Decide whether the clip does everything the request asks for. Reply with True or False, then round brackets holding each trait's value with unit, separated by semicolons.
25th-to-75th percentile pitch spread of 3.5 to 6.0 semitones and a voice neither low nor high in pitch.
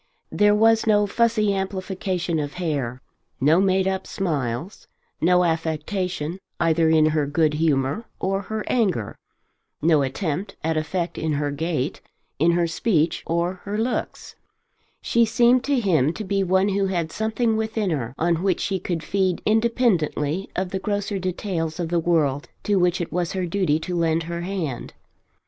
True (3.9 semitones; 180 Hz)